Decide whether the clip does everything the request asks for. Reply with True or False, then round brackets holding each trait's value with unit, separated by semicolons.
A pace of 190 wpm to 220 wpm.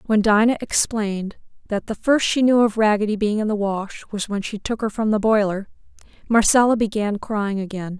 True (195 wpm)